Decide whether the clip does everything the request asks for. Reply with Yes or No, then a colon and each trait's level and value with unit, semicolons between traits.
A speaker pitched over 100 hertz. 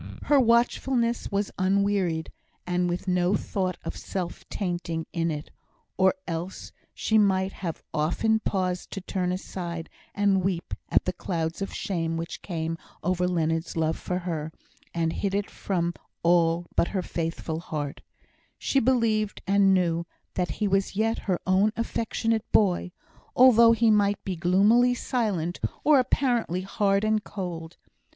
Yes: medium, 185 Hz